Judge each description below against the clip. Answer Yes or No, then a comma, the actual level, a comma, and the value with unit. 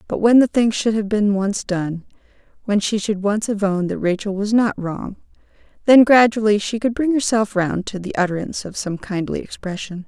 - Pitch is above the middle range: Yes, high, 205 Hz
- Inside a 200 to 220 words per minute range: Yes, fast, 205 wpm